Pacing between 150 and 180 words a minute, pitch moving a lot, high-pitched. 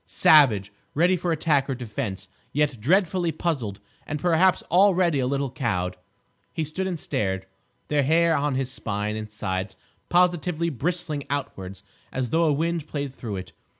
No: average, 155 wpm; wide, 7.3 semitones; medium, 145 Hz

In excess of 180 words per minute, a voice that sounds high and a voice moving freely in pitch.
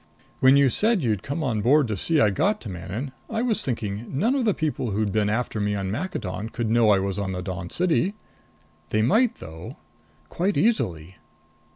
No: average, 200 wpm; low, 115 Hz; wide, 8.6 semitones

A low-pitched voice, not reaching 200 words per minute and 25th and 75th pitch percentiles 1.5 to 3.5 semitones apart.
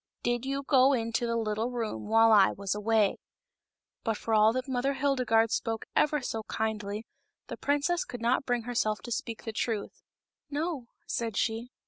No: high, 230 Hz; average, 180 wpm; average, 2.7 semitones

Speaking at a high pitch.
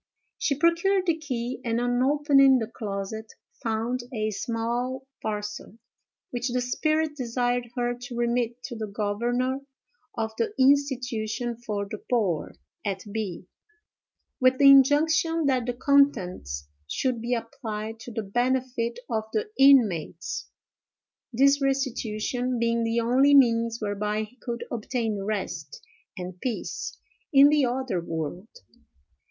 Yes: high, 240 Hz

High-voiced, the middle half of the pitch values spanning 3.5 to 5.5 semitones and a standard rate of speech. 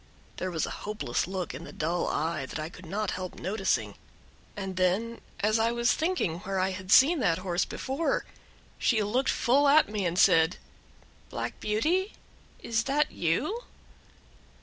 Yes: high, 195 Hz; average, 5.1 semitones; average, 165 wpm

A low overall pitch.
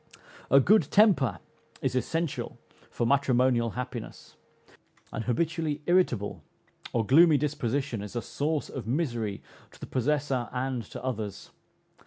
Yes: low, 130 Hz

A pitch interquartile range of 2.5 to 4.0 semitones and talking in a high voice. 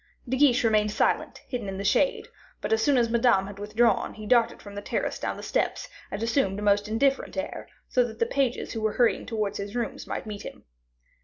Yes: average, 2.9 semitones; high, 225 Hz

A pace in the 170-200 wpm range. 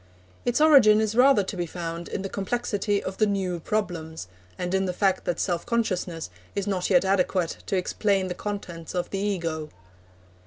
Yes: average, 185 wpm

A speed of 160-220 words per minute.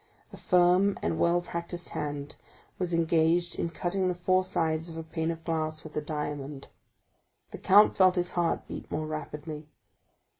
Yes: average, 165 wpm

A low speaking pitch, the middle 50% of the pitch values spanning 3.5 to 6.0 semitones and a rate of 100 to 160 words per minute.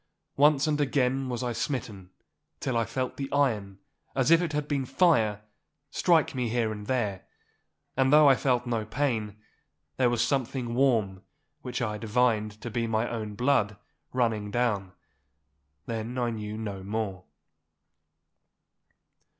Yes: low, 120 Hz; average, 3.8 semitones; average, 140 wpm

